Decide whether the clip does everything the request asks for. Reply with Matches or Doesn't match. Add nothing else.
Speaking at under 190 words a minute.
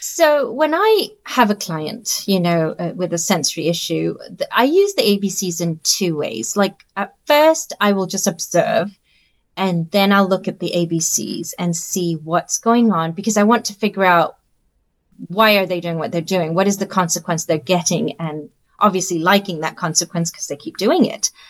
Doesn't match